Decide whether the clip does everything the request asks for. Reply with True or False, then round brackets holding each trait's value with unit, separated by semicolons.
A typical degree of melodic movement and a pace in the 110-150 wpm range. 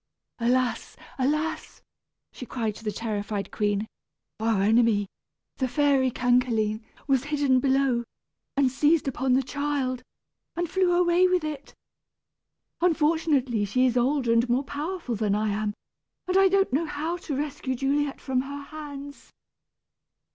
True (4.1 semitones; 140 wpm)